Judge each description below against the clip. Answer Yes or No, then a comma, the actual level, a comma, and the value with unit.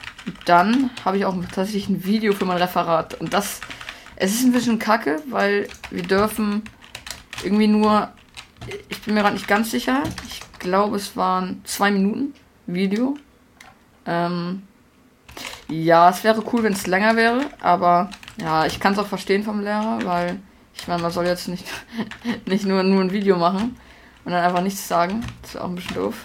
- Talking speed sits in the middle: Yes, average, 180 wpm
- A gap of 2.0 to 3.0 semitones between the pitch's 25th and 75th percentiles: No, average, 3.5 semitones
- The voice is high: Yes, high, 200 Hz